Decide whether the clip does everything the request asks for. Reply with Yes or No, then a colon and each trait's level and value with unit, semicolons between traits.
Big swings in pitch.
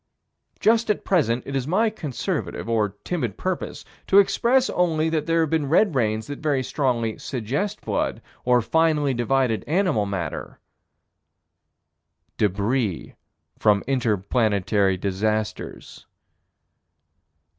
Yes: wide, 7.0 semitones